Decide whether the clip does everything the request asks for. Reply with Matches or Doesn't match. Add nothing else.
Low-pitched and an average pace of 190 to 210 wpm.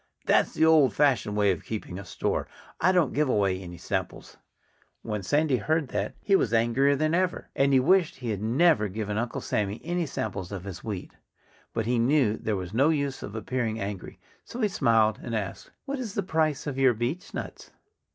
Matches